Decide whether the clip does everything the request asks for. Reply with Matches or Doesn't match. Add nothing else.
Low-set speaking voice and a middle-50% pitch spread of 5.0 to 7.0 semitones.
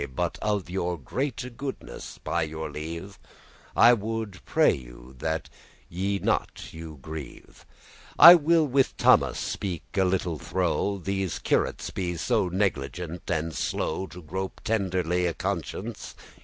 Doesn't match